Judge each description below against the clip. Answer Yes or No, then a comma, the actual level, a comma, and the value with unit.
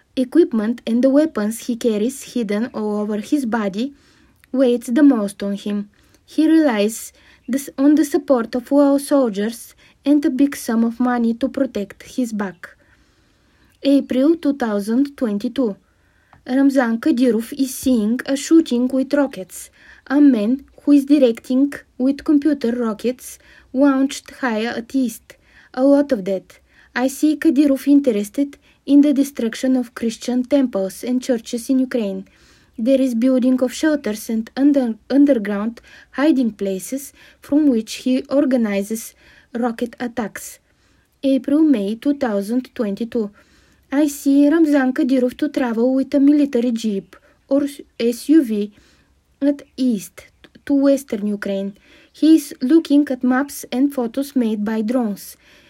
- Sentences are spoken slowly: Yes, slow, 130 wpm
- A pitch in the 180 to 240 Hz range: No, very high, 260 Hz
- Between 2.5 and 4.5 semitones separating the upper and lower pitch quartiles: Yes, average, 3.6 semitones